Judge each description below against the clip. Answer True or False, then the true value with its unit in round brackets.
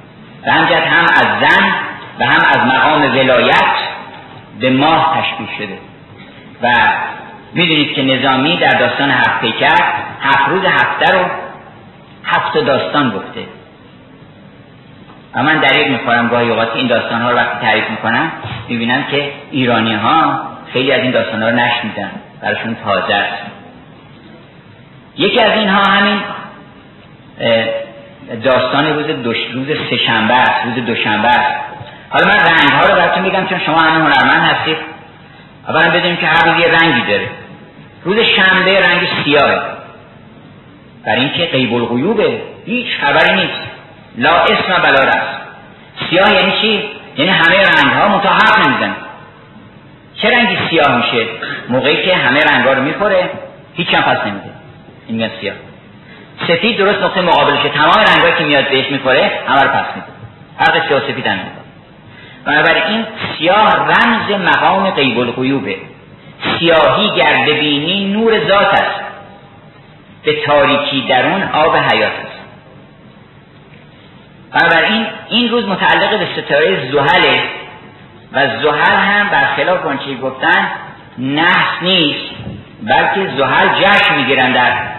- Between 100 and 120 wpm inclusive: False (130 wpm)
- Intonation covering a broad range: True (7.0 semitones)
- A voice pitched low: False (155 Hz)